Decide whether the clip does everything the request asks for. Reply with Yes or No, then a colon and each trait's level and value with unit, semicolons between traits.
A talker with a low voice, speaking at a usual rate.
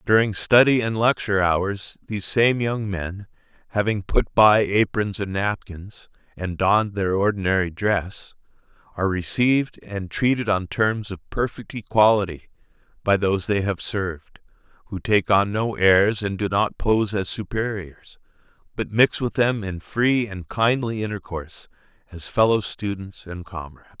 Yes: low, 100 Hz; average, 150 wpm